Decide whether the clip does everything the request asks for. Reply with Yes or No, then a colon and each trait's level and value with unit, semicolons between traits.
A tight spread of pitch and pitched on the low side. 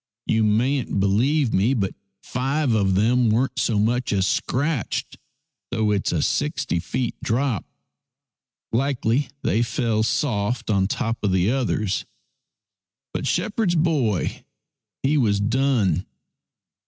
No: average, 4.5 semitones; low, 115 Hz